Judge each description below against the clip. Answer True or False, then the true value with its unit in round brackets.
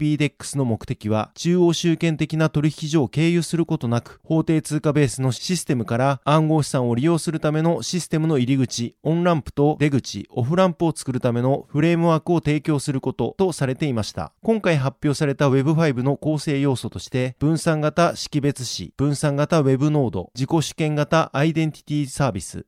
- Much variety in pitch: False (3.6 semitones)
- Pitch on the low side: False (150 Hz)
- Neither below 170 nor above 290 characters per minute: False (400 characters per minute)